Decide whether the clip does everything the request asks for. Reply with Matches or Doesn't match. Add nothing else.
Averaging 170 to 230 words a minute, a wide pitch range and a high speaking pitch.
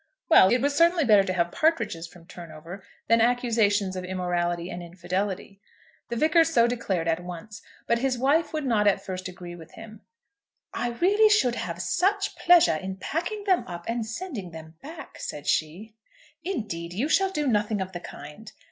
Matches